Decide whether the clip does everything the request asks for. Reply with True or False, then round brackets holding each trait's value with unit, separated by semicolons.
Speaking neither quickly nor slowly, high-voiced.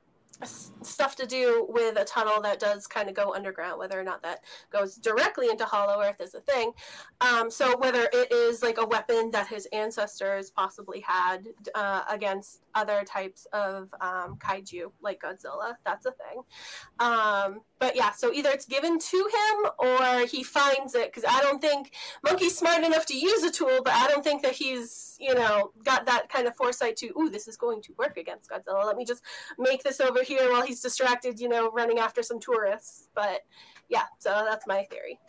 True (195 wpm; 245 Hz)